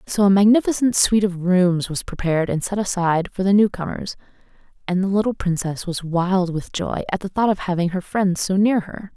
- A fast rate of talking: Yes, fast, 215 wpm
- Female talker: Yes, female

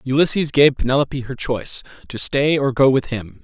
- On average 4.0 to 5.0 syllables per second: No, 5.5 syllables/s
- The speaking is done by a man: Yes, male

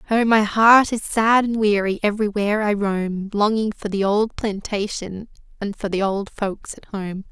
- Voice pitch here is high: Yes, high, 205 Hz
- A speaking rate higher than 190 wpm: No, average, 180 wpm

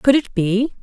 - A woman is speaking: Yes, female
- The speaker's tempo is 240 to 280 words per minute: No, fast, 220 wpm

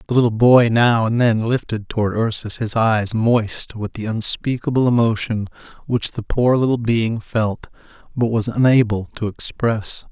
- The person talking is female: No, male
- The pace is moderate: Yes, average, 160 wpm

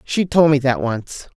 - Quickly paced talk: Yes, fast, 215 wpm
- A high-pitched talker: No, medium, 145 Hz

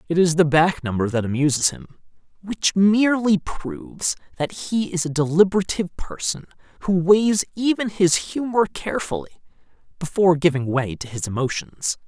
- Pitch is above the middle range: No, medium, 170 Hz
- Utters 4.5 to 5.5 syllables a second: Yes, 5.1 syllables/s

